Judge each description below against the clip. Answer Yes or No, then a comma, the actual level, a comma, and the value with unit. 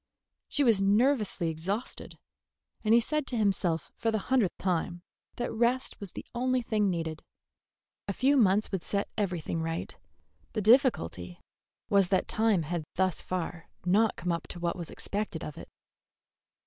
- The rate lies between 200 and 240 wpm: No, average, 160 wpm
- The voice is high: Yes, high, 195 Hz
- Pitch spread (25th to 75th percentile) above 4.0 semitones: Yes, average, 4.8 semitones